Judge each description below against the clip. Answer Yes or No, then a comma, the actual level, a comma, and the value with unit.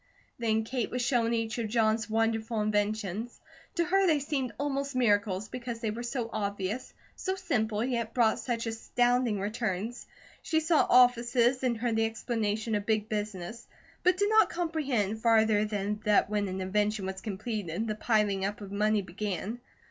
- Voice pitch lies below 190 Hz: No, high, 225 Hz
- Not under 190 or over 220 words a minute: No, average, 165 wpm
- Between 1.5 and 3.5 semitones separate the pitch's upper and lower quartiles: Yes, average, 2.7 semitones